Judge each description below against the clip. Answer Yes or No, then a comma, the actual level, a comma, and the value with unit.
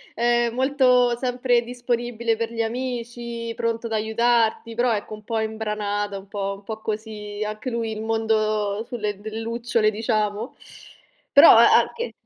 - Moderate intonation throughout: No, narrow, 1.9 semitones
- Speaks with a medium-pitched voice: No, high, 225 Hz